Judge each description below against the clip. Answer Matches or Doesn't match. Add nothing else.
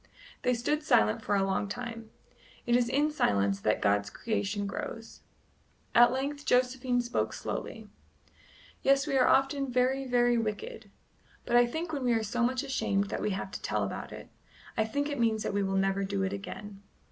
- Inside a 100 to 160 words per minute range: Doesn't match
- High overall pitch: Matches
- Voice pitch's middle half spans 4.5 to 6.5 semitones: Matches